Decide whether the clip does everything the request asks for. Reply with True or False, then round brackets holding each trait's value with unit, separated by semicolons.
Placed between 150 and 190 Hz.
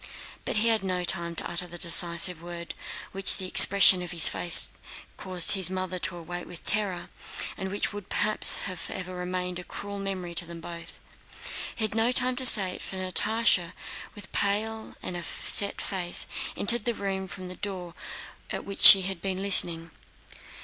True (185 Hz)